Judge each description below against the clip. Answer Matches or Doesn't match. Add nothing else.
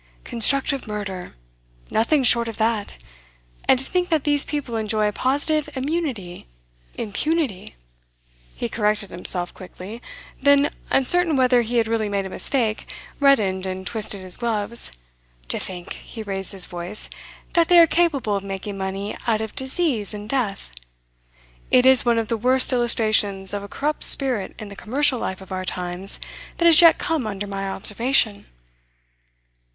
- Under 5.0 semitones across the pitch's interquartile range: Doesn't match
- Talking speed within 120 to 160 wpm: Matches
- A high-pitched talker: Matches